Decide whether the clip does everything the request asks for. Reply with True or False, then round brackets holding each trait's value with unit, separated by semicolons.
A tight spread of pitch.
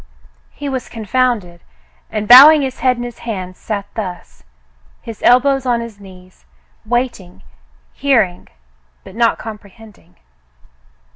False (4.7 semitones)